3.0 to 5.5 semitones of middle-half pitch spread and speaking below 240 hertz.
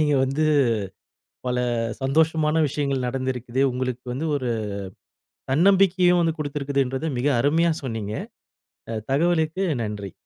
Yes: average, 4.1 semitones; medium, 140 Hz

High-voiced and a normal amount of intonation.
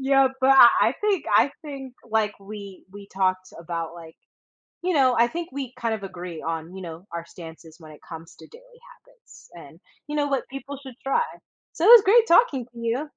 No: high, 240 Hz; wide, 8.1 semitones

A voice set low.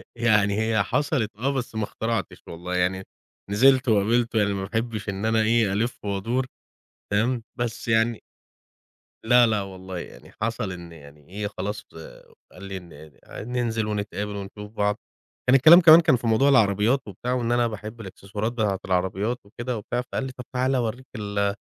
Yes: low, 110 Hz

